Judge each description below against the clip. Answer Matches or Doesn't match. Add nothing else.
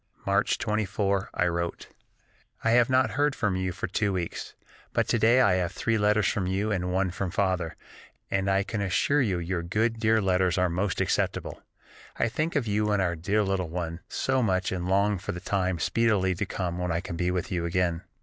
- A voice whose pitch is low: Matches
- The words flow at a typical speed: Doesn't match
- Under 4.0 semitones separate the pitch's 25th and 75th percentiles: Matches